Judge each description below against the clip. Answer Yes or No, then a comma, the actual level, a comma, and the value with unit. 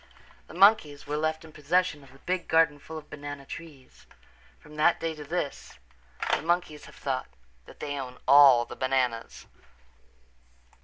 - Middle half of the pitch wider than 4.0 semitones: No, average, 2.9 semitones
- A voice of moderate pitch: Yes, medium, 150 Hz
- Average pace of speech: Yes, average, 160 wpm